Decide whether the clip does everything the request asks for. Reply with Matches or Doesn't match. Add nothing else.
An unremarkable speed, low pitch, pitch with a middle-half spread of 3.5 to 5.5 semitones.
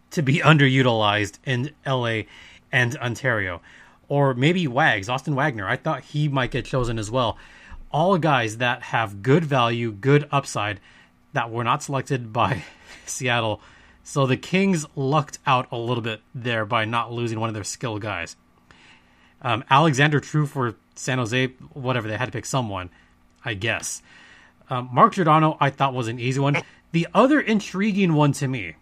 Matches